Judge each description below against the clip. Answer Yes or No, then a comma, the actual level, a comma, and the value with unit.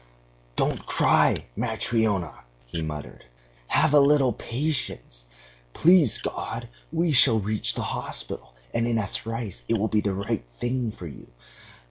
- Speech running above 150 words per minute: No, average, 140 wpm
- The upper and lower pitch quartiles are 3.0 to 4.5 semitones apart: No, average, 5.1 semitones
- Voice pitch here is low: Yes, low, 110 Hz